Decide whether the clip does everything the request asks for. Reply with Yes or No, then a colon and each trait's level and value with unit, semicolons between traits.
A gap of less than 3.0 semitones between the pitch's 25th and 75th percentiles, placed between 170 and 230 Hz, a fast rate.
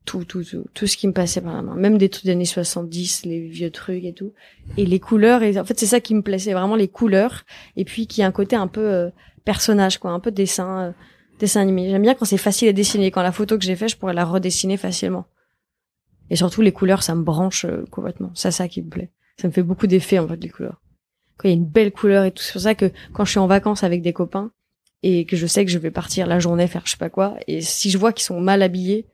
Yes: narrow, 2.4 semitones; high, 190 Hz; fast, 280 wpm